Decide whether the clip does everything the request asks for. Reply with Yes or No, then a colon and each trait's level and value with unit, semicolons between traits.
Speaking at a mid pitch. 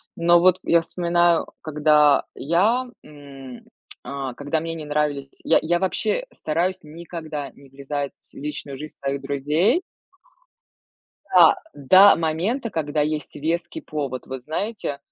Yes: medium, 155 Hz